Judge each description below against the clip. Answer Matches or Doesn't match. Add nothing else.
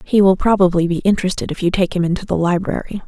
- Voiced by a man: Doesn't match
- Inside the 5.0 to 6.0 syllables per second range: Doesn't match